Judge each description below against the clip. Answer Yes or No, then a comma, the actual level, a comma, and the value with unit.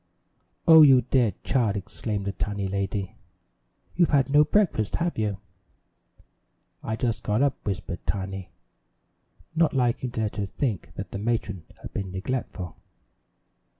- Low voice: Yes, low, 110 Hz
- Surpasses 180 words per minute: No, average, 140 wpm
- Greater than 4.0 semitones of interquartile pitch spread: Yes, average, 5.1 semitones